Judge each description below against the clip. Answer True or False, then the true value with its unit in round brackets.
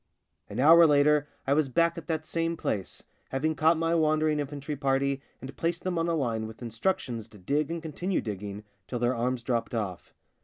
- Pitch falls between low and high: True (145 Hz)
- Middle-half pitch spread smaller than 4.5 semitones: False (5.2 semitones)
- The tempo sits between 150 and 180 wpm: False (200 wpm)